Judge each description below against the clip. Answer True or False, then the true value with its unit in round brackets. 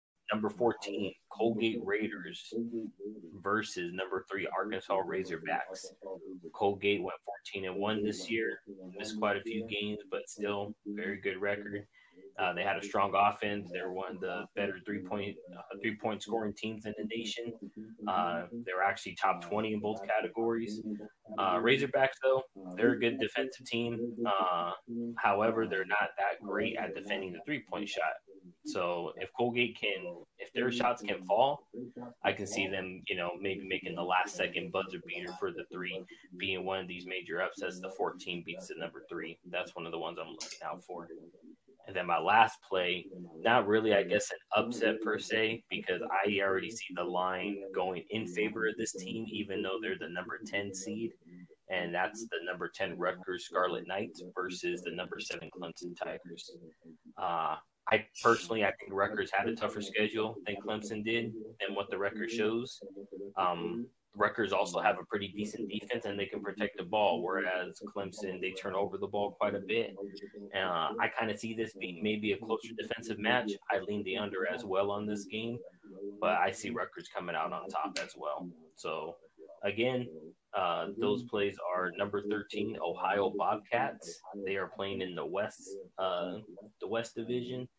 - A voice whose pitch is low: True (105 Hz)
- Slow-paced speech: False (175 wpm)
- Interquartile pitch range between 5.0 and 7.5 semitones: False (2.7 semitones)